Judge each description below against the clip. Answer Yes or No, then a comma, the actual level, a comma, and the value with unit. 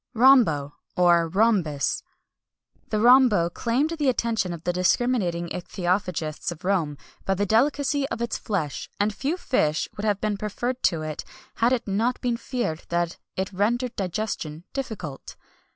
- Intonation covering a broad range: Yes, wide, 5.9 semitones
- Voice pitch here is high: Yes, high, 205 Hz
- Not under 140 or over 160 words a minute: Yes, average, 150 wpm